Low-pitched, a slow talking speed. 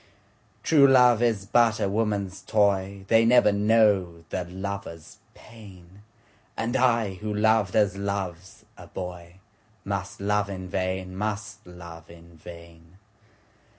Yes: low, 100 Hz; slow, 115 wpm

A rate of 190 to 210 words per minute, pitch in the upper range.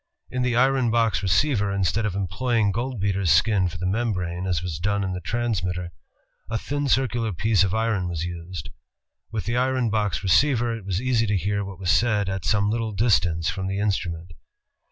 No: average, 195 wpm; low, 100 Hz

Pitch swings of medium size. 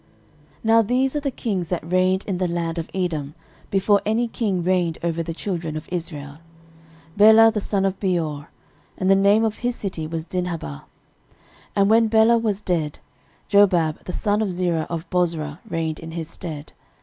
Yes: average, 4.0 semitones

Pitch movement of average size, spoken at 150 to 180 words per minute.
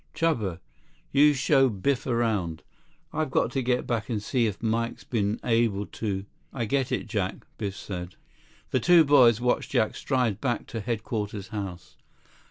Yes: average, 3.9 semitones; average, 160 wpm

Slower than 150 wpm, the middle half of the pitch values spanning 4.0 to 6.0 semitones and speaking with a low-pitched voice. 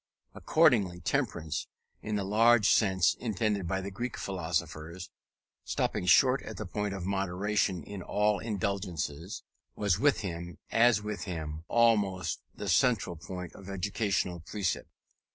No: slow, 135 wpm; average, 3.2 semitones; low, 100 Hz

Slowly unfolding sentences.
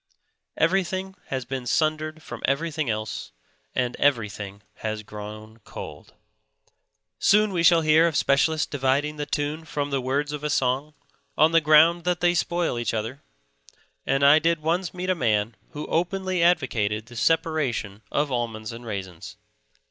No: average, 155 wpm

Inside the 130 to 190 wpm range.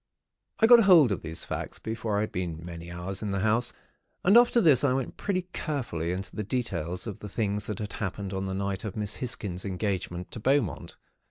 No: fast, 205 wpm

